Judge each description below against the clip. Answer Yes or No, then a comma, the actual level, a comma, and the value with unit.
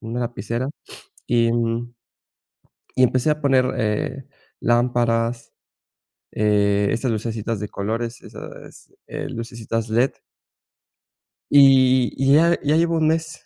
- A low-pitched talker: Yes, low, 120 Hz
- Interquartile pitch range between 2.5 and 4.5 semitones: Yes, average, 2.8 semitones